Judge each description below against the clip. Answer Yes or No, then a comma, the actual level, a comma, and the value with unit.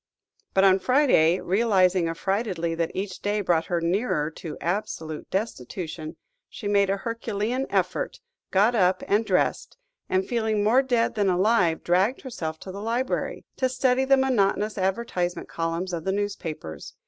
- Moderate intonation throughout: Yes, average, 4.7 semitones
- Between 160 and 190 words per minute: No, average, 150 wpm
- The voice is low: No, high, 195 Hz